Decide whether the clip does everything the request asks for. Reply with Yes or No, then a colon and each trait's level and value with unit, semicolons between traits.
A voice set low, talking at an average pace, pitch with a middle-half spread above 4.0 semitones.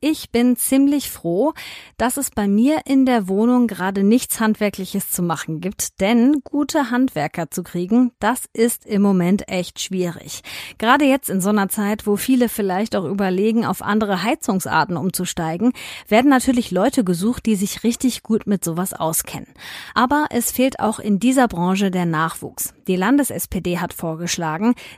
No: high, 210 Hz; average, 160 wpm; average, 5.0 semitones